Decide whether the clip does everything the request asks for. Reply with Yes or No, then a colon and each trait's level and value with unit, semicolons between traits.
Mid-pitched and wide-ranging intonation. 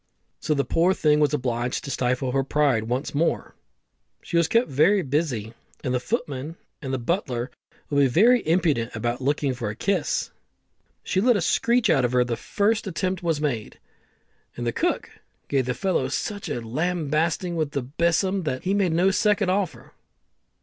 Yes: medium, 150 Hz; wide, 6.3 semitones